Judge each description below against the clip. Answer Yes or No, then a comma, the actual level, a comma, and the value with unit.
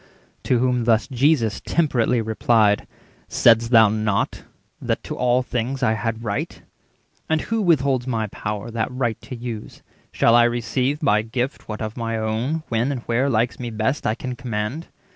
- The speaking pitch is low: Yes, low, 120 Hz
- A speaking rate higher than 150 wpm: Yes, average, 175 wpm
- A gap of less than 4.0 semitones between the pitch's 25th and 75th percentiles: Yes, narrow, 2.6 semitones